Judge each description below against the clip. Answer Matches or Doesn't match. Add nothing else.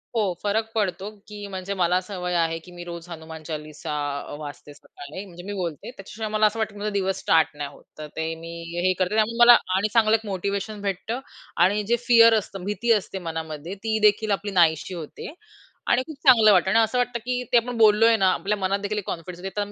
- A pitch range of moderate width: Matches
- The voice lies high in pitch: Matches